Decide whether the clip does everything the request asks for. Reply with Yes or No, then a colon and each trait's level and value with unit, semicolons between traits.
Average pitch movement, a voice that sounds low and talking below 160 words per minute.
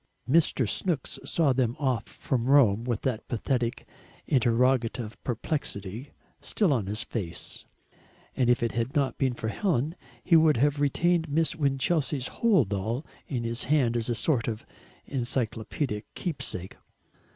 Yes: average, 4.0 semitones; low, 125 Hz; average, 140 wpm